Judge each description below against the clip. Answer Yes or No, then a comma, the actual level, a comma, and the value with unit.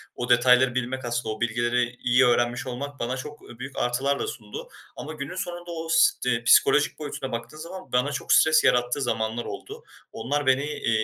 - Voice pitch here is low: Yes, low, 125 Hz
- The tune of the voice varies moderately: Yes, average, 3.1 semitones